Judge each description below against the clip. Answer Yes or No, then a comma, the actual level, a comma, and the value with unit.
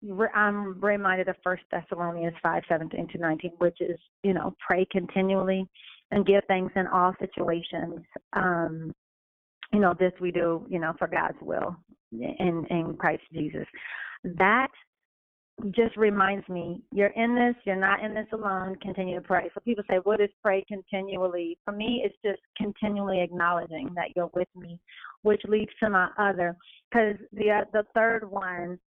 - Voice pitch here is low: No, high, 190 Hz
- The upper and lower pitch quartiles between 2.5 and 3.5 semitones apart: Yes, average, 2.8 semitones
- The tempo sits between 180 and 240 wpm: No, average, 160 wpm